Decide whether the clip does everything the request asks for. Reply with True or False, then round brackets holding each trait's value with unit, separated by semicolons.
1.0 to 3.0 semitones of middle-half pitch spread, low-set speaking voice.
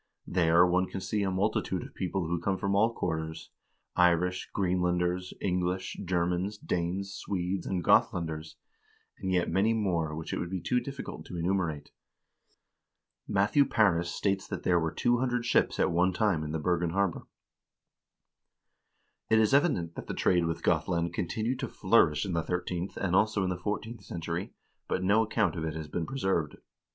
True (2.7 semitones; 90 Hz)